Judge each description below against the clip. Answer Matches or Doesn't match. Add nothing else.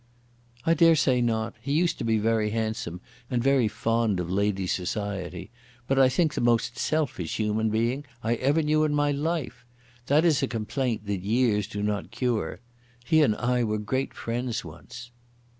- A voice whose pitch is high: Doesn't match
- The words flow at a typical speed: Matches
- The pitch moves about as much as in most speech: Matches